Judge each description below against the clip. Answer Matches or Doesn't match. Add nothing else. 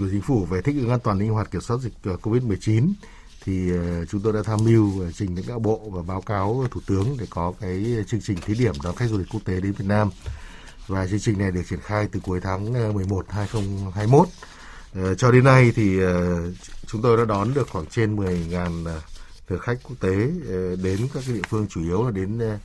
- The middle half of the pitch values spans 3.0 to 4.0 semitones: Matches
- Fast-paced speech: Doesn't match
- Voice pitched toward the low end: Matches